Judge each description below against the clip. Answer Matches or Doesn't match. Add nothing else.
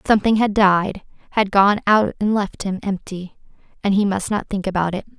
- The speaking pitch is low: Doesn't match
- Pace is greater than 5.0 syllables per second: Matches